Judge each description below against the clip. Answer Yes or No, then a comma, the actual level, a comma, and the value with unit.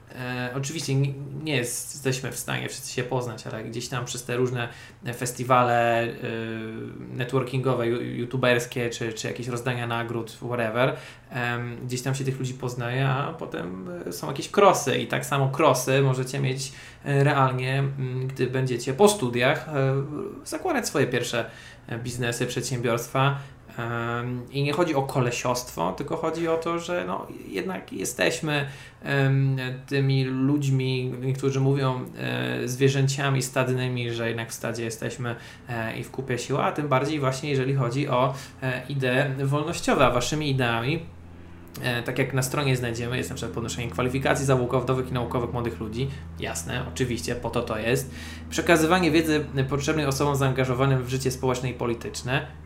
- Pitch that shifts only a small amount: Yes, narrow, 2.2 semitones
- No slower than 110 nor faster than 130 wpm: No, average, 145 wpm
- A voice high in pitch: No, low, 130 Hz